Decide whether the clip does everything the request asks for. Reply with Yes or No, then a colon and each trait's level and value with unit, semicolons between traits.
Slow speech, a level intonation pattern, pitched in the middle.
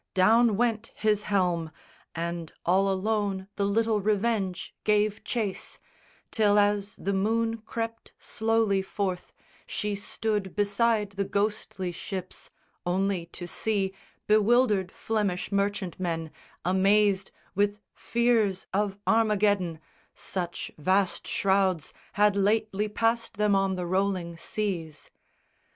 No: slow, 110 wpm; narrow, 2.2 semitones; high, 200 Hz